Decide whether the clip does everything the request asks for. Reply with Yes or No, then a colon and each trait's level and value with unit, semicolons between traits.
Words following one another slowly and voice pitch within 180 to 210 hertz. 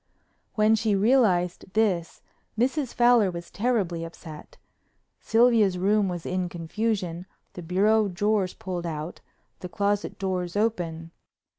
Yes: slow, 120 wpm; high, 190 Hz